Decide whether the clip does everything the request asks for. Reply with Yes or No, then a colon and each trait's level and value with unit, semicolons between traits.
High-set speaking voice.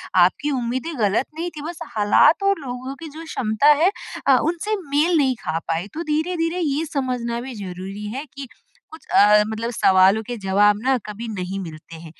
Yes: very high, 250 Hz